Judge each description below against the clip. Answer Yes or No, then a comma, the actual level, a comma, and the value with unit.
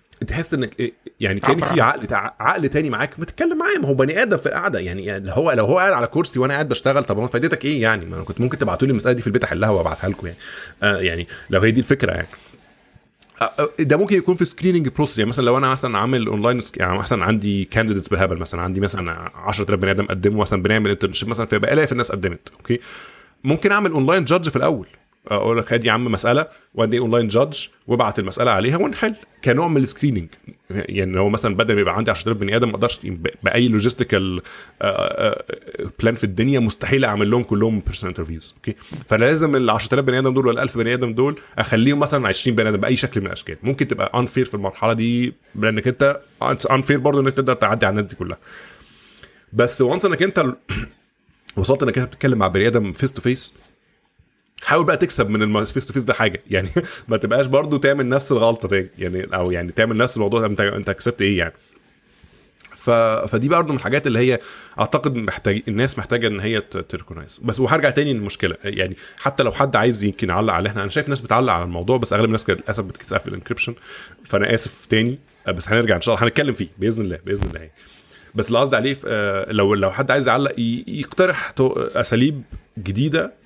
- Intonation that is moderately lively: Yes, average, 4.8 semitones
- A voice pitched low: Yes, low, 115 Hz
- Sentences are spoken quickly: Yes, fast, 205 wpm